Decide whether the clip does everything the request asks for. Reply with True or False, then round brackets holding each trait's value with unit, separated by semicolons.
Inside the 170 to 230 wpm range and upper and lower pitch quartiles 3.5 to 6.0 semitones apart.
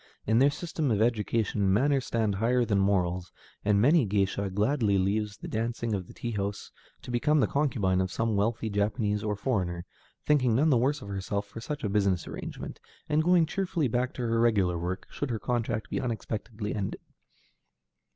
True (190 wpm; 3.8 semitones)